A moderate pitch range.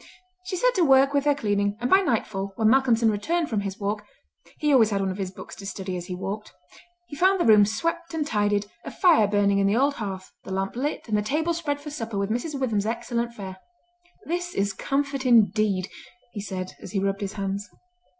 No: wide, 6.2 semitones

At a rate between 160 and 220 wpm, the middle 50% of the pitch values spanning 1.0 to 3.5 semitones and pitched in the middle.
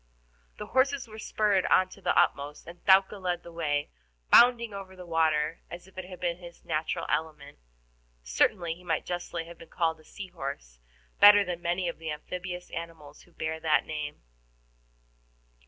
Yes: average, 175 wpm; average, 2.8 semitones; medium, 170 Hz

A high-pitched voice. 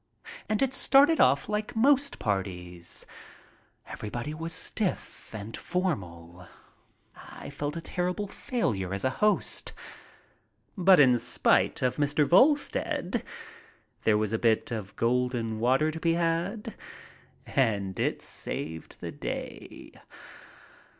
No: medium, 140 Hz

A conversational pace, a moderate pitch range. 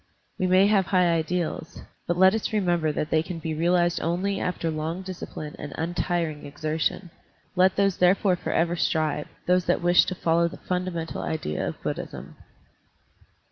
No: average, 175 wpm; narrow, 2.3 semitones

